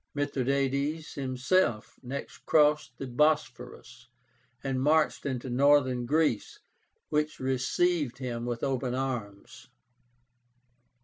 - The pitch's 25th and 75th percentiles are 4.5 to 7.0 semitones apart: No, average, 3.1 semitones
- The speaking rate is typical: No, slow, 90 wpm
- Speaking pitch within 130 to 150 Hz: Yes, low, 135 Hz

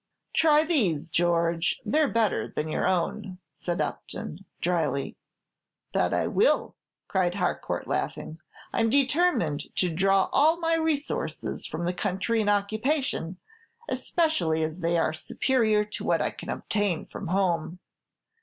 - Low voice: No, high, 190 Hz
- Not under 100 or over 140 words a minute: Yes, slow, 135 wpm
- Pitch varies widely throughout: Yes, wide, 7.4 semitones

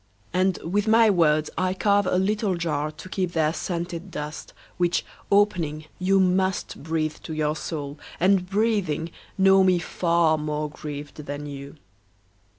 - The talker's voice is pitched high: No, medium, 170 Hz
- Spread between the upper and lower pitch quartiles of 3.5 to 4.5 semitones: Yes, average, 3.8 semitones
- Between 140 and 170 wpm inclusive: Yes, average, 150 wpm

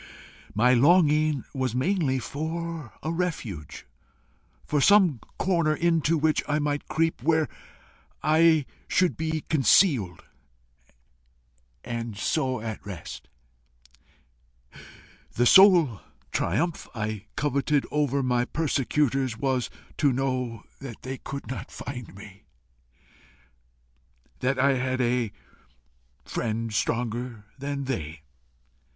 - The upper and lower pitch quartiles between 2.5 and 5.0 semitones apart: Yes, average, 4.7 semitones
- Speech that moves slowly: Yes, slow, 100 wpm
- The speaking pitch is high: No, low, 135 Hz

